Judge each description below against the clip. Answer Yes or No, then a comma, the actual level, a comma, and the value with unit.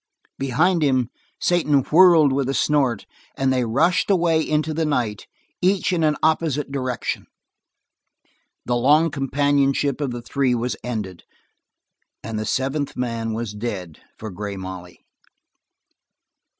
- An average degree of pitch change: Yes, average, 4.5 semitones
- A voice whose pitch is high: No, low, 135 Hz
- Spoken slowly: Yes, slow, 130 wpm